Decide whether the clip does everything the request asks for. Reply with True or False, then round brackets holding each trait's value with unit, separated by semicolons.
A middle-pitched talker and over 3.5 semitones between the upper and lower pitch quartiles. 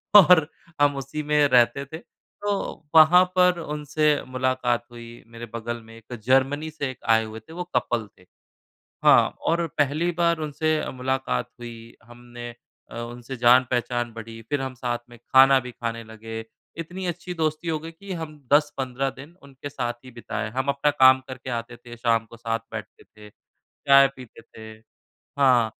False (130 Hz; 4.3 semitones)